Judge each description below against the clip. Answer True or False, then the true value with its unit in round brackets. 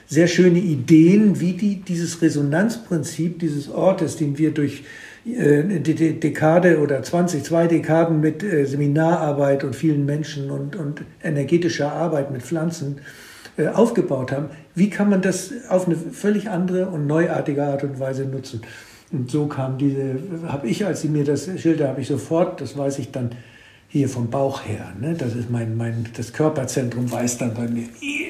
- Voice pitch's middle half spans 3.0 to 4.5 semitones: True (3.5 semitones)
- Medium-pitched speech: True (150 Hz)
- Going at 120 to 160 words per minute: False (175 wpm)